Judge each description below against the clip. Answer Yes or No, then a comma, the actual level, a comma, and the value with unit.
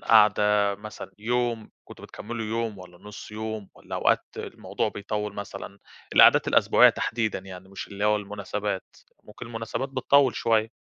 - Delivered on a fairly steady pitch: Yes, narrow, 1.9 semitones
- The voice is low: Yes, low, 105 Hz